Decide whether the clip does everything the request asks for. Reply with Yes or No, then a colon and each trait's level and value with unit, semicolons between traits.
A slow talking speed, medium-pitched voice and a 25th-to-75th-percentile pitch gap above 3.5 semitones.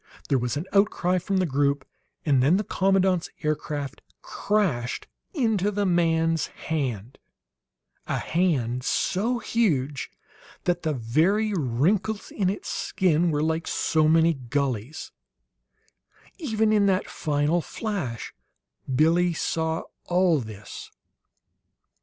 Yes: slow, 115 wpm; medium, 165 Hz; average, 5.3 semitones